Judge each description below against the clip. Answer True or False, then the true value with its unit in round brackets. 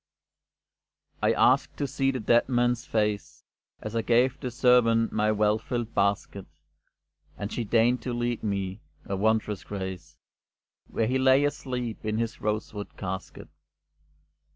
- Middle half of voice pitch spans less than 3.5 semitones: True (2.9 semitones)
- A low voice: True (115 Hz)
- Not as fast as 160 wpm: True (140 wpm)